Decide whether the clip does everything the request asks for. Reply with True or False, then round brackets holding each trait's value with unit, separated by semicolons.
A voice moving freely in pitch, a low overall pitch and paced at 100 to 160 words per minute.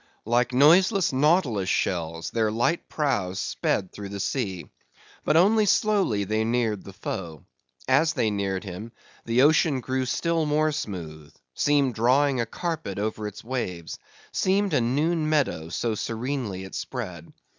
True (7.1 semitones; 120 Hz; 145 wpm)